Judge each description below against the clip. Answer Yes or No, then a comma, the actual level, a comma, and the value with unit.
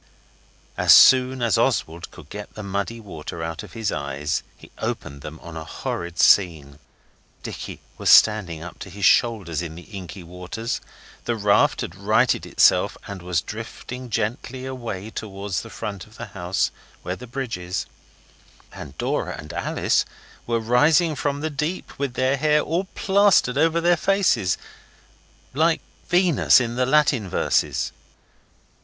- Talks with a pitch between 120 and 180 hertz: No, low, 110 Hz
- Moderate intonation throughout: No, wide, 6.7 semitones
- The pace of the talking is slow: No, average, 155 wpm